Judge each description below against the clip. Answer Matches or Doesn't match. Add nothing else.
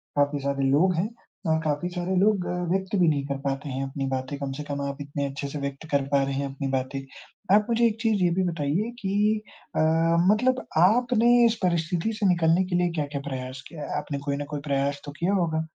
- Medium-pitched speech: Matches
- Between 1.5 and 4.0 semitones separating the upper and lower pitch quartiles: Doesn't match